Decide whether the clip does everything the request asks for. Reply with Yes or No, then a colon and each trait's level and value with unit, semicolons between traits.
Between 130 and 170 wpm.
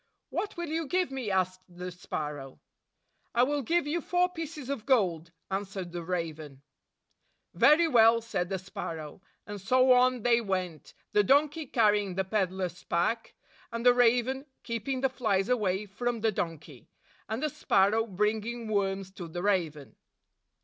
Yes: average, 155 wpm